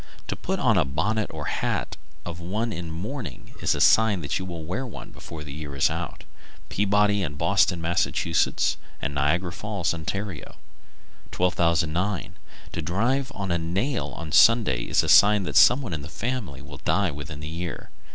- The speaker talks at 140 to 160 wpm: No, average, 175 wpm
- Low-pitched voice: Yes, very low, 85 Hz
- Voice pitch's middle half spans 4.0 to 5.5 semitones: Yes, average, 4.7 semitones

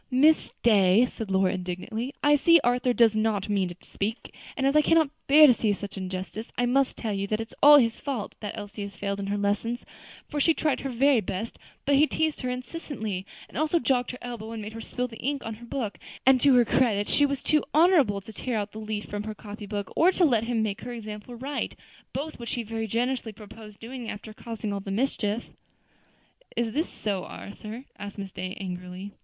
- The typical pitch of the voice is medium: No, high, 225 Hz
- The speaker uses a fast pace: Yes, fast, 225 wpm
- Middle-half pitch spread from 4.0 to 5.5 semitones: Yes, average, 4.3 semitones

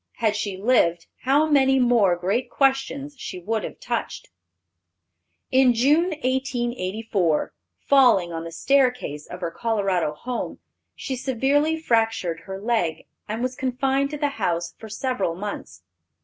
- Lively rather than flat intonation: Yes, wide, 6.3 semitones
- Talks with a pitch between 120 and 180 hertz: No, high, 235 Hz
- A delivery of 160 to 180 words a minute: No, slow, 135 wpm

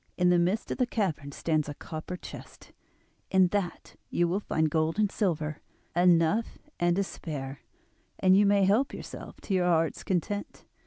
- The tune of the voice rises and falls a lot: No, average, 3.8 semitones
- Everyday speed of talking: Yes, average, 170 wpm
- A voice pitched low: No, medium, 175 Hz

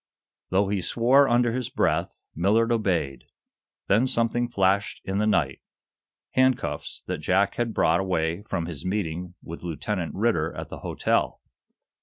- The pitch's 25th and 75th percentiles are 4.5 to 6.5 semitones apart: Yes, average, 5.2 semitones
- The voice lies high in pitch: No, low, 100 Hz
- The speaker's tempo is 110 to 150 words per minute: Yes, average, 145 wpm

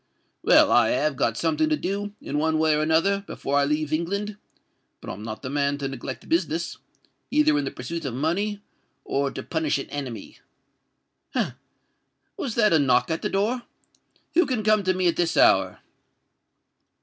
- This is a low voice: No, medium, 165 Hz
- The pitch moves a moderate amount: No, wide, 6.3 semitones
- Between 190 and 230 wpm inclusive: No, average, 175 wpm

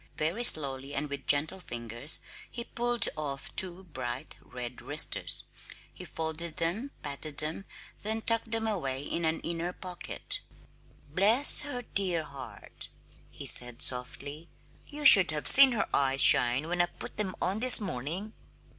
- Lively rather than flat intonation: Yes, wide, 6.9 semitones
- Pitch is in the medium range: Yes, medium, 165 Hz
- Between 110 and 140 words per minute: No, average, 150 wpm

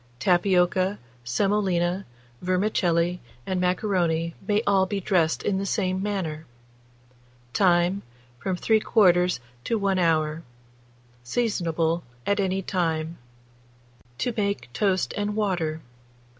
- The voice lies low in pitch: No, medium, 185 Hz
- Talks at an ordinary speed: No, slow, 100 wpm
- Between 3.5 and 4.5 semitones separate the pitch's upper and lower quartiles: No, average, 3.0 semitones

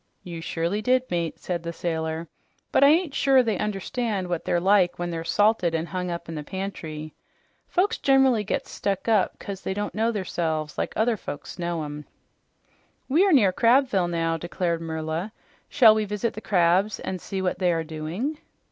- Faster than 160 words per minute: Yes, average, 185 wpm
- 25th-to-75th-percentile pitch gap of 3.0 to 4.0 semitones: No, average, 4.7 semitones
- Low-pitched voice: No, medium, 185 Hz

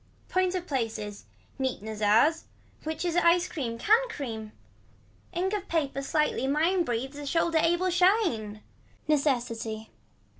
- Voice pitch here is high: Yes, very high, 295 Hz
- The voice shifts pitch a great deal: Yes, wide, 7.3 semitones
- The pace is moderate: No, slow, 125 wpm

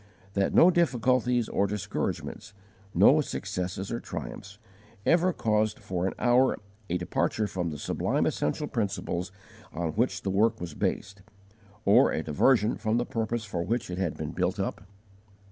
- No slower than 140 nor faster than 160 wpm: Yes, average, 155 wpm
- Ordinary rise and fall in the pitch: Yes, average, 4.6 semitones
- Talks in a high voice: No, low, 105 Hz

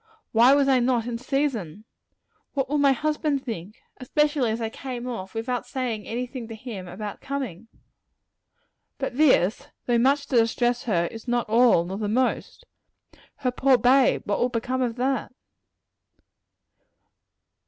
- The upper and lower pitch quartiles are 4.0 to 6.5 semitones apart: No, average, 3.0 semitones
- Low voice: No, high, 245 Hz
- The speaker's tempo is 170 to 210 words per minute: No, average, 155 wpm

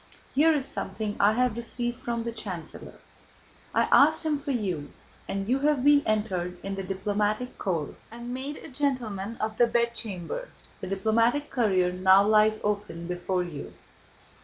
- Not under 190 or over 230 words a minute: No, average, 160 wpm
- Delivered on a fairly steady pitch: No, average, 4.5 semitones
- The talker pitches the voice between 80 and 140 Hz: No, high, 215 Hz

